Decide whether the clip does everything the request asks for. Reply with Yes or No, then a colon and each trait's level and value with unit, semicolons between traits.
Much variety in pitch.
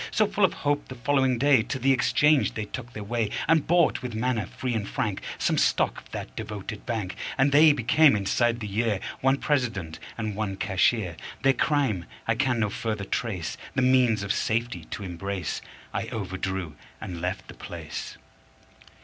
No: average, 4.9 semitones